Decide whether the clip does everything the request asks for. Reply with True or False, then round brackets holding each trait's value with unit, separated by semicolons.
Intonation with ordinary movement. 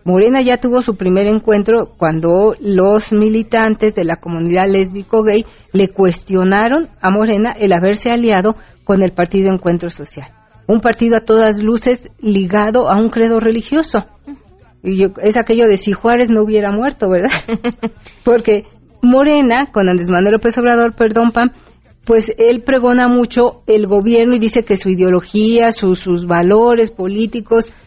True (3.3 semitones)